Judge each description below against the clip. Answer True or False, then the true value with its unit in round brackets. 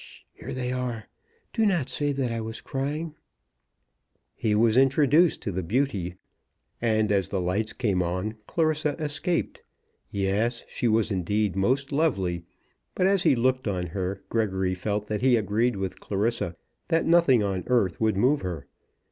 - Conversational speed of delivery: True (160 wpm)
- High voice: False (115 Hz)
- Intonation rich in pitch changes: True (5.7 semitones)